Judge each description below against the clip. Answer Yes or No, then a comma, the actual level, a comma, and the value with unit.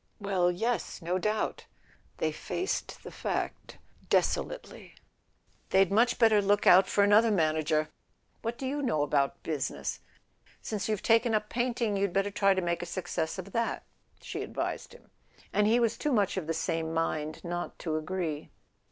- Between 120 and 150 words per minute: No, average, 170 wpm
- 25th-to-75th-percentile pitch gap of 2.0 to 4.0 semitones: No, average, 5.1 semitones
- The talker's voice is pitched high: Yes, high, 195 Hz